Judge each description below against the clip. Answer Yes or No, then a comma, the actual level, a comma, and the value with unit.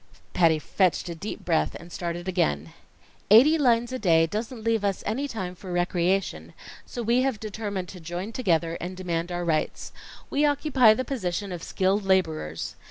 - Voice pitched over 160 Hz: Yes, high, 190 Hz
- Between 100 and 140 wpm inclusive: No, average, 170 wpm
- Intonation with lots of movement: No, average, 4.7 semitones